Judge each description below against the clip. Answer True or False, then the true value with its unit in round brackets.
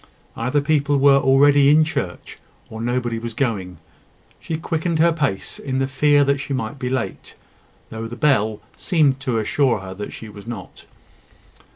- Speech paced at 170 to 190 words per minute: True (175 wpm)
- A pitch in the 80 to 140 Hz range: True (135 Hz)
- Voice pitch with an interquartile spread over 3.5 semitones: True (4.2 semitones)